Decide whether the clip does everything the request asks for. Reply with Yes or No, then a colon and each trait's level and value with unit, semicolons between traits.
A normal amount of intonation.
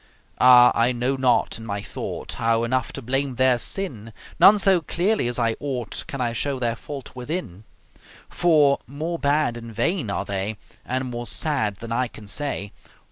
Yes: average, 3.7 semitones